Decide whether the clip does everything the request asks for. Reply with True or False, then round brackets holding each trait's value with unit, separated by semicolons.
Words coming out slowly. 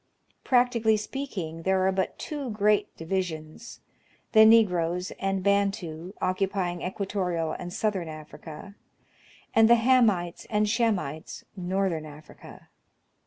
True (115 wpm)